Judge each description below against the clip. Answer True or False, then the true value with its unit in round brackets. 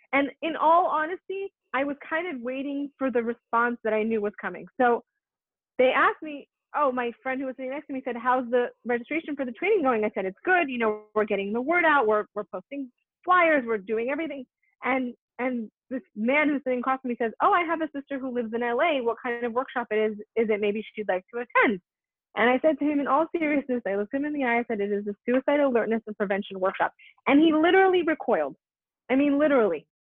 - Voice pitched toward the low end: False (255 Hz)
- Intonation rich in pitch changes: False (4.5 semitones)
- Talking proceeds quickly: True (235 wpm)